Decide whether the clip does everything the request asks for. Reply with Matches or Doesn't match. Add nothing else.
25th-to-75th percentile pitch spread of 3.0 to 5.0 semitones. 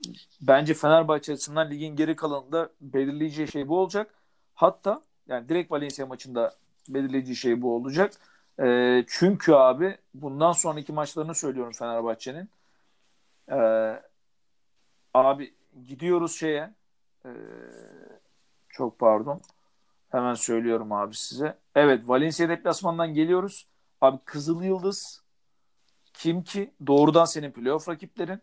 Matches